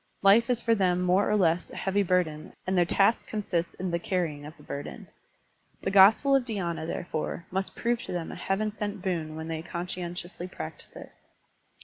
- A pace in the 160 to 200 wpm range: Yes, average, 195 wpm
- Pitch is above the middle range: No, medium, 180 Hz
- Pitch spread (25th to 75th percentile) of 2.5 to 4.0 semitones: Yes, average, 3.0 semitones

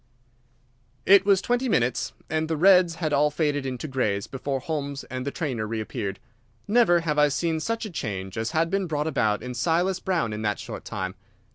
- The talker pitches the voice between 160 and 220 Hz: No, medium, 150 Hz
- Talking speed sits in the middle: Yes, average, 190 wpm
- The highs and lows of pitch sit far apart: Yes, wide, 5.9 semitones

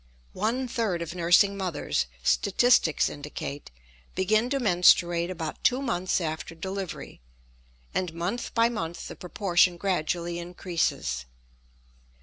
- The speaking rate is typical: No, slow, 115 wpm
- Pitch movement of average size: Yes, average, 3.2 semitones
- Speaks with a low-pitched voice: No, medium, 180 Hz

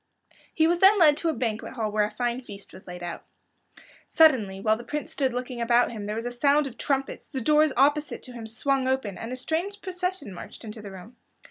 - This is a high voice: Yes, very high, 250 Hz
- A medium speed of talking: No, fast, 230 wpm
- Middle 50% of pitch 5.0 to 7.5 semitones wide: Yes, wide, 5.5 semitones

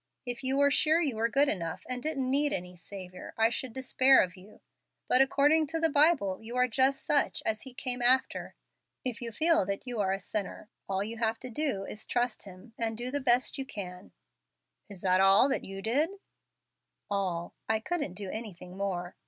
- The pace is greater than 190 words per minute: Yes, average, 200 wpm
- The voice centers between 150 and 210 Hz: No, high, 230 Hz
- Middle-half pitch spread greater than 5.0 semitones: Yes, wide, 5.5 semitones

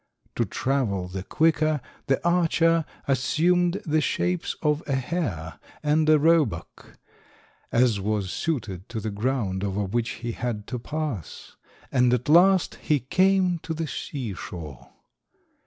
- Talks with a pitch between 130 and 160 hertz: Yes, low, 135 Hz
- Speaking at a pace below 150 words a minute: Yes, average, 140 wpm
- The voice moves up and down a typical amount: No, wide, 7.4 semitones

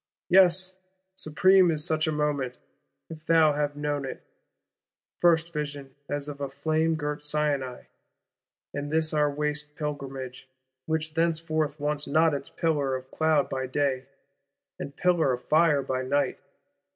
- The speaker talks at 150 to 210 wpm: No, average, 140 wpm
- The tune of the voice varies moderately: No, narrow, 2.2 semitones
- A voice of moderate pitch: Yes, medium, 150 Hz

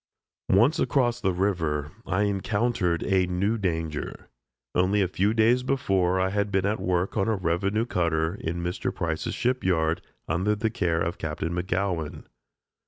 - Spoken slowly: No, average, 160 wpm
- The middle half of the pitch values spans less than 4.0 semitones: Yes, average, 3.3 semitones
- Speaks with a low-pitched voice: Yes, very low, 95 Hz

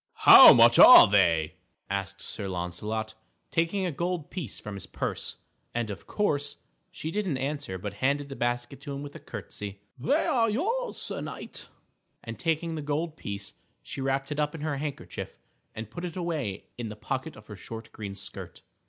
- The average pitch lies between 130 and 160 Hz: Yes, low, 135 Hz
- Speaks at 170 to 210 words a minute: Yes, average, 190 wpm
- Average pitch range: No, wide, 7.3 semitones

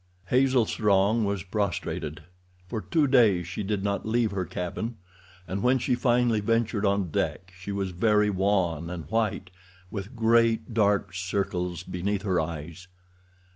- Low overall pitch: Yes, low, 100 Hz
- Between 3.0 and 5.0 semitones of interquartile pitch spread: Yes, average, 3.7 semitones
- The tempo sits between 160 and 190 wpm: No, average, 145 wpm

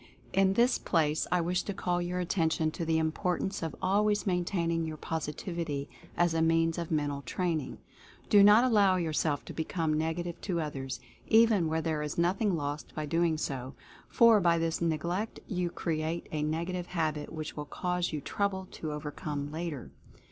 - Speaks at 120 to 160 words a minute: No, average, 175 wpm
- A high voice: No, medium, 165 Hz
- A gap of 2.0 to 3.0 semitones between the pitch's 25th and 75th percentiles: Yes, narrow, 2.6 semitones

